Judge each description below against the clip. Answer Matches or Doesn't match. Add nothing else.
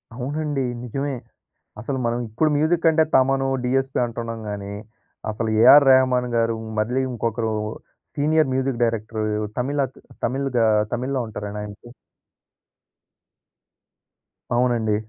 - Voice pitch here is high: Doesn't match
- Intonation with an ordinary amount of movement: Matches